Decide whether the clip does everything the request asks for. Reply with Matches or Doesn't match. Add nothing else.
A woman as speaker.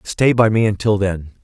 Doesn't match